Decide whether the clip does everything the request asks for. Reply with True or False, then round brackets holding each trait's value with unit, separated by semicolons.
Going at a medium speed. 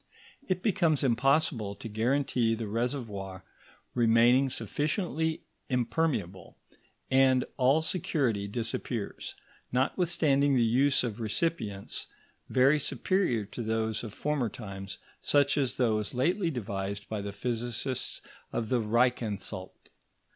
False (110 wpm)